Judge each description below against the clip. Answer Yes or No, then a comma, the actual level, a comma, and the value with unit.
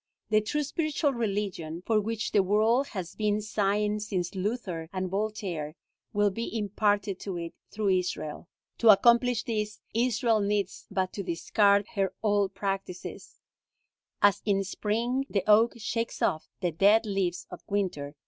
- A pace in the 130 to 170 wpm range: Yes, average, 150 wpm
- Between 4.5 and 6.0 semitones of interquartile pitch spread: No, narrow, 2.6 semitones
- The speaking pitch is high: Yes, high, 205 Hz